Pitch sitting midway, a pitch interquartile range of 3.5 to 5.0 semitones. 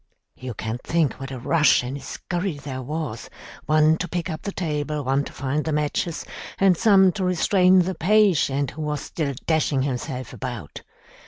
Yes: medium, 150 Hz; average, 4.6 semitones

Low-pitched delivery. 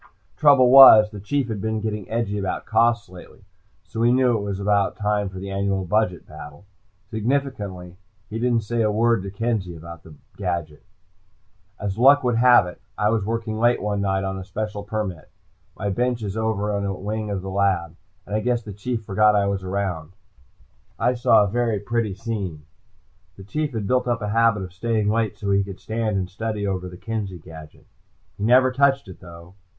Yes: low, 105 Hz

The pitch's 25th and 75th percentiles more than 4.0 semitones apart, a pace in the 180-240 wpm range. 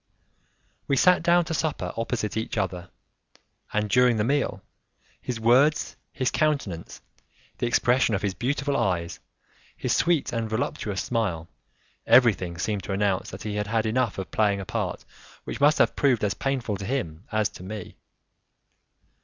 No: average, 4.7 semitones; average, 160 wpm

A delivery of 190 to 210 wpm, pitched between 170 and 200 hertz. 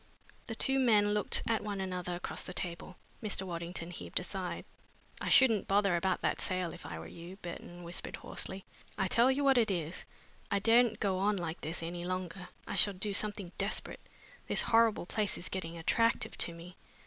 Yes: average, 195 wpm; high, 190 Hz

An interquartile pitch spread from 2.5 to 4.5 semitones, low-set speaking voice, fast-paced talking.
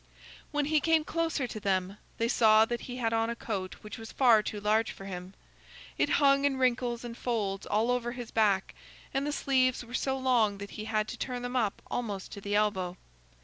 No: average, 3.6 semitones; high, 230 Hz; fast, 215 wpm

